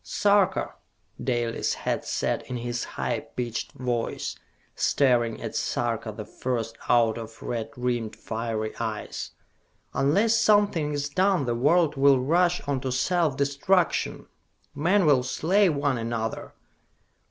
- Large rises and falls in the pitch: Yes, wide, 6.2 semitones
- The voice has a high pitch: No, low, 135 Hz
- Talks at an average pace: No, slow, 130 wpm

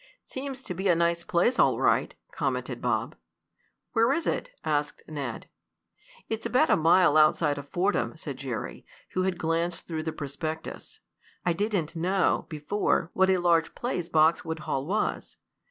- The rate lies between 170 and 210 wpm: No, average, 155 wpm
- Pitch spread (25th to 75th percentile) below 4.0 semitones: Yes, average, 3.4 semitones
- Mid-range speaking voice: Yes, medium, 170 Hz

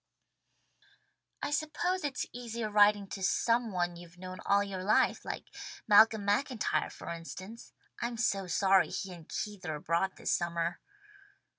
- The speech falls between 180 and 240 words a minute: No, average, 145 wpm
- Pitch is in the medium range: No, high, 200 Hz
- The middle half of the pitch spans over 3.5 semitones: Yes, average, 4.3 semitones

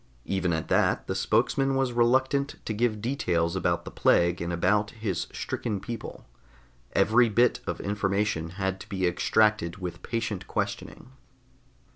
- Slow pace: No, average, 145 wpm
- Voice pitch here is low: Yes, low, 105 Hz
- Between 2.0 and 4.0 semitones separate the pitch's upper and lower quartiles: No, average, 4.6 semitones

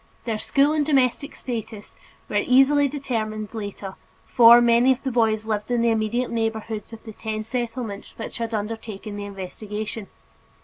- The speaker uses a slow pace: No, average, 160 wpm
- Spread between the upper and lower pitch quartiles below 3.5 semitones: Yes, narrow, 2.4 semitones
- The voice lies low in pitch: No, high, 225 Hz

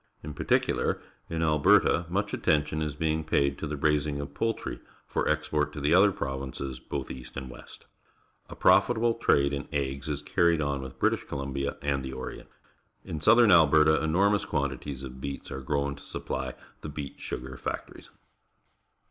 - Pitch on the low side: Yes, very low, 70 Hz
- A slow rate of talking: No, average, 170 wpm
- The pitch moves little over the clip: Yes, narrow, 2.3 semitones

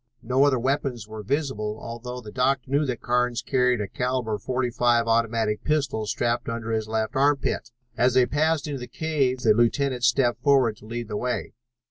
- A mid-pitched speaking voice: No, low, 125 Hz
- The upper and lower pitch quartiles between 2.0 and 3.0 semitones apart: Yes, average, 2.7 semitones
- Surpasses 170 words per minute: Yes, average, 180 wpm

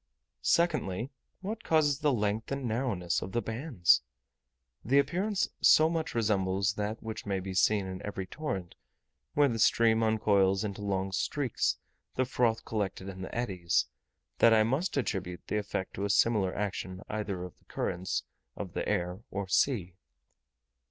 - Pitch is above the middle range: No, low, 105 Hz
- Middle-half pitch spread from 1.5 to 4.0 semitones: No, average, 4.7 semitones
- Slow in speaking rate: No, average, 160 wpm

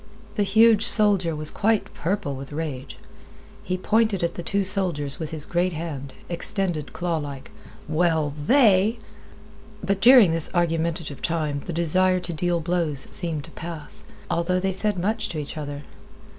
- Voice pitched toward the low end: No, medium, 170 Hz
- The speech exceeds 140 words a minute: Yes, average, 155 wpm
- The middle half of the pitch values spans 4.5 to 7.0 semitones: No, average, 3.9 semitones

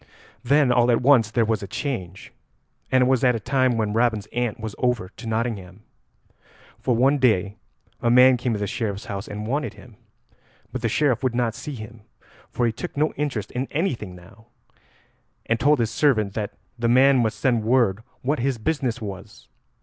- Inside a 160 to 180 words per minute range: No, average, 190 wpm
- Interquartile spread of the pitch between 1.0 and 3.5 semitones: Yes, average, 3.2 semitones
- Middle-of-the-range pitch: No, low, 120 Hz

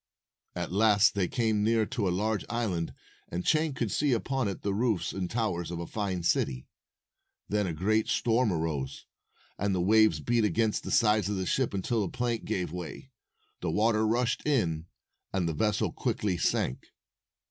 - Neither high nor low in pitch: No, low, 105 Hz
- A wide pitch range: No, average, 4.2 semitones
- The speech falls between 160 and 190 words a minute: Yes, average, 180 wpm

